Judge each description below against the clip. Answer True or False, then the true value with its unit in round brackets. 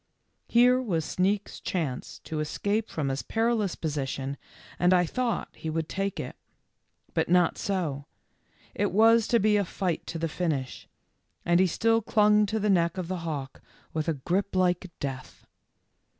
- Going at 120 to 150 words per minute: False (165 wpm)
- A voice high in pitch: False (180 Hz)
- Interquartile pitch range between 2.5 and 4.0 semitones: False (4.8 semitones)